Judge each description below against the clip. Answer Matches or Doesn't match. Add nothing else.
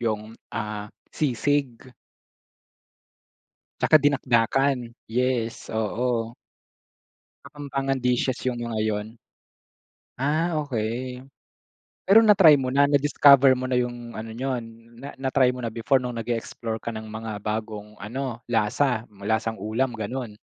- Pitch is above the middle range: Doesn't match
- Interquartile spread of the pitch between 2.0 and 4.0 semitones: Matches